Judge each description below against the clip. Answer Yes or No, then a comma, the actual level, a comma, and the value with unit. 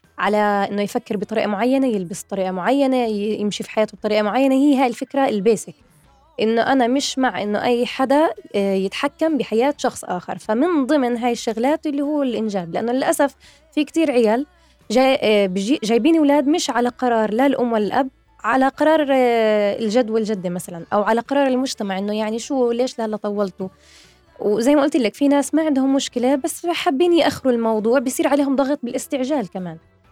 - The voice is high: Yes, high, 245 Hz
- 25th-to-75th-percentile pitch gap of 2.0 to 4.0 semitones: No, average, 4.7 semitones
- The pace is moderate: No, fast, 165 wpm